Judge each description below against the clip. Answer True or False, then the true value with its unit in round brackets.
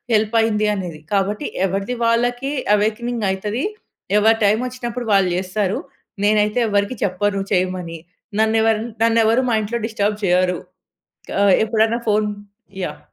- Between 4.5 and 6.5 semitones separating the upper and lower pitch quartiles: False (2.6 semitones)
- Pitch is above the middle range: True (210 Hz)